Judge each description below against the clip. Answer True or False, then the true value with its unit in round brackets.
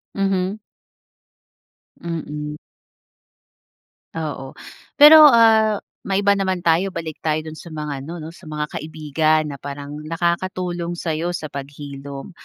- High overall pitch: False (160 Hz)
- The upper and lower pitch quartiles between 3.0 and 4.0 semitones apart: True (3.7 semitones)